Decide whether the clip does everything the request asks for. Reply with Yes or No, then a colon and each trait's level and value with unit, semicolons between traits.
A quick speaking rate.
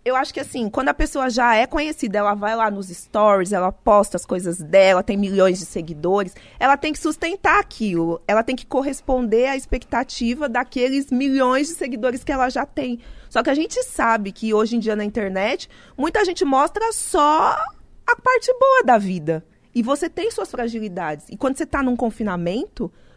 Yes: fast, 190 wpm